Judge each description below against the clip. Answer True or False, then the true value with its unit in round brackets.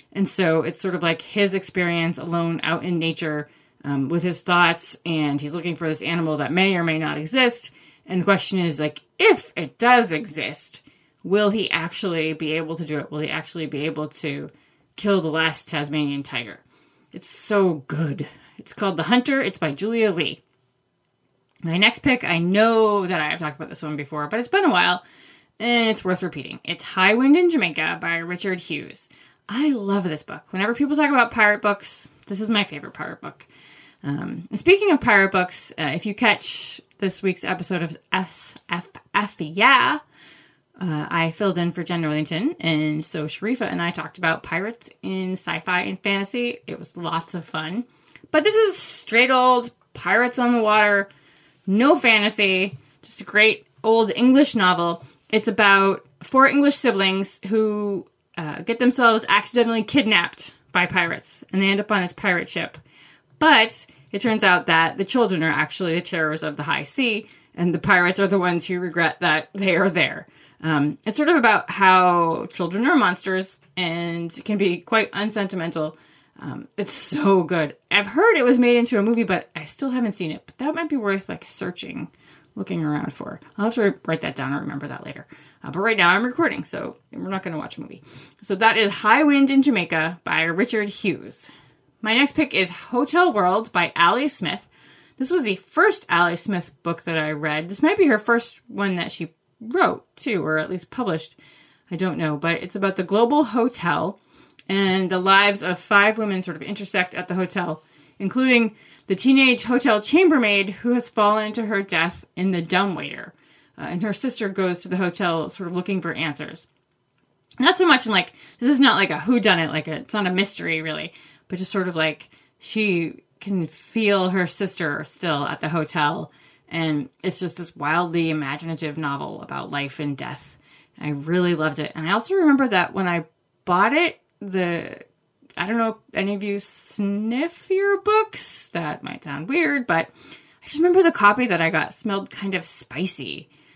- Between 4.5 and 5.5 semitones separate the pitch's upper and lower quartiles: True (5.2 semitones)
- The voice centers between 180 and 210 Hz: True (185 Hz)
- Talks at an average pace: True (190 wpm)